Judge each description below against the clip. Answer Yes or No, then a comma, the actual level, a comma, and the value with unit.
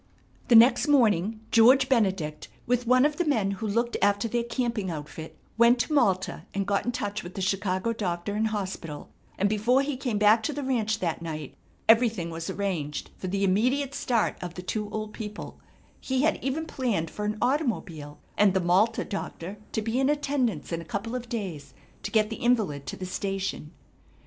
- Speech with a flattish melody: No, average, 4.5 semitones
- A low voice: No, high, 210 Hz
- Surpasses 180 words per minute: Yes, average, 195 wpm